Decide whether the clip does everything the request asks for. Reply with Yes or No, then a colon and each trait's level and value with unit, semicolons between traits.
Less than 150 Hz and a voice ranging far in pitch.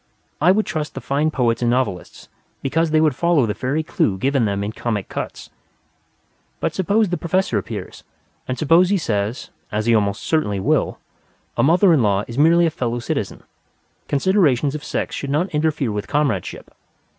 Yes: medium, 140 Hz; wide, 6.1 semitones